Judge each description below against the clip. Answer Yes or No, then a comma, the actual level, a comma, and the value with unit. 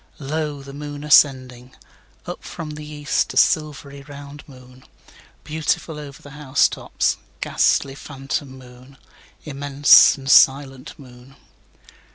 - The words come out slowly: Yes, slow, 105 wpm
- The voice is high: No, medium, 140 Hz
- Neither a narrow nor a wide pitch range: No, narrow, 1.7 semitones